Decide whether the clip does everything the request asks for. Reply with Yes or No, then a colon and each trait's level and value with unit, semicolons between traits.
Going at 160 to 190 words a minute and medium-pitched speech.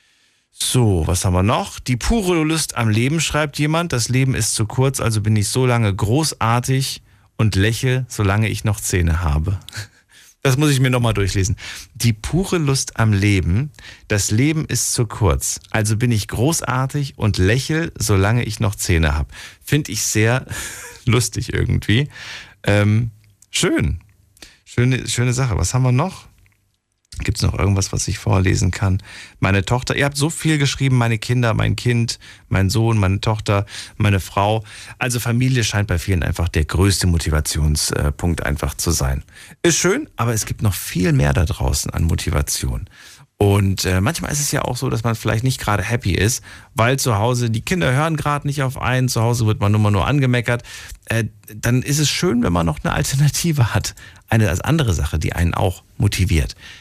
No: average, 180 wpm; low, 110 Hz